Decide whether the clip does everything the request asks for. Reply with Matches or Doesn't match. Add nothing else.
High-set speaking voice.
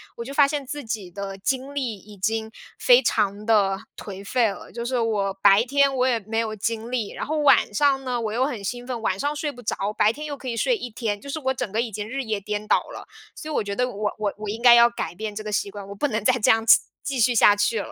Matches